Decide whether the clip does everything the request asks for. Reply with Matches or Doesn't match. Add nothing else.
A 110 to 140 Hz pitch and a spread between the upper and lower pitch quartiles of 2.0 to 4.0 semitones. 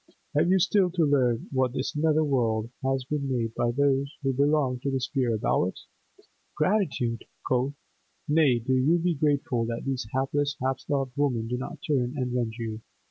Matches